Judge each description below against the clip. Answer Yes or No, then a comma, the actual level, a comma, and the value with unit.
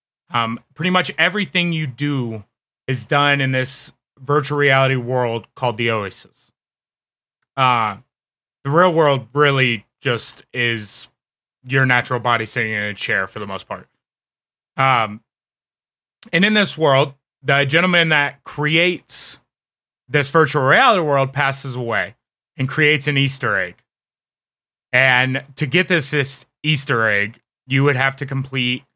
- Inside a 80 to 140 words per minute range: Yes, slow, 135 wpm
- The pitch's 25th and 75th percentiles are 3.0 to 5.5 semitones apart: Yes, average, 3.3 semitones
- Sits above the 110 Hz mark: Yes, low, 135 Hz